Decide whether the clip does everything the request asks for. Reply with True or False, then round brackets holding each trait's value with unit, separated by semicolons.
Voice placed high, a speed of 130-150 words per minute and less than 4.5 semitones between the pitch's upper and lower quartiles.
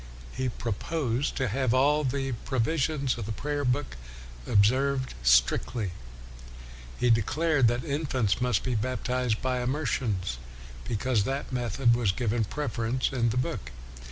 False (125 Hz; 140 wpm; 3.1 semitones)